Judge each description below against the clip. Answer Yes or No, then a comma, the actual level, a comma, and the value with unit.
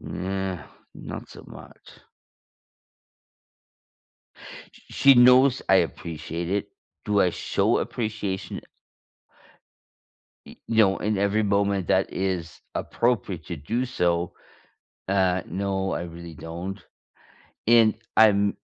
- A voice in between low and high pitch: No, very low, 95 Hz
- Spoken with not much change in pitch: No, average, 3.5 semitones